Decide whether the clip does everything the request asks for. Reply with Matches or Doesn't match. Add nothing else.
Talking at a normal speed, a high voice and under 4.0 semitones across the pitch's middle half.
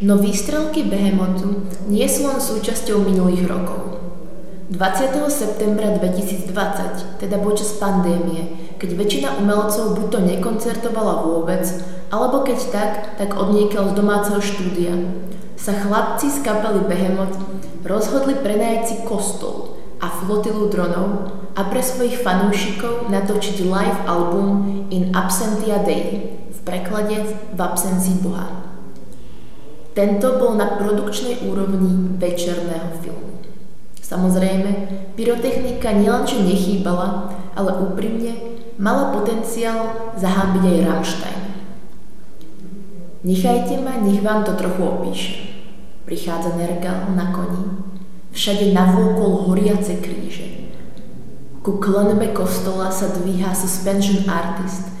Doesn't match